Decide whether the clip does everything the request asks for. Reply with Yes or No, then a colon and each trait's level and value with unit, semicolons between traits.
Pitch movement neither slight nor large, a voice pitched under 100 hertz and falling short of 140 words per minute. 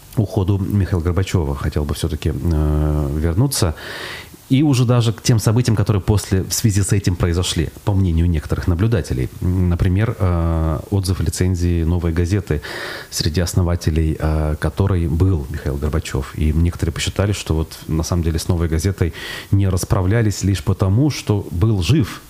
No: average, 4.0 semitones; very low, 90 Hz; average, 145 wpm